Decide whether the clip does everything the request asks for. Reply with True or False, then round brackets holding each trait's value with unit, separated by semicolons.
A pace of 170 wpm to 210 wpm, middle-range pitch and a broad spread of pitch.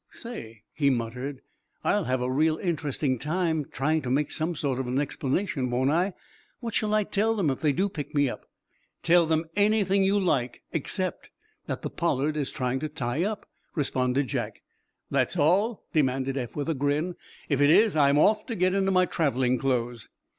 True (190 wpm; 150 Hz; 5.7 semitones)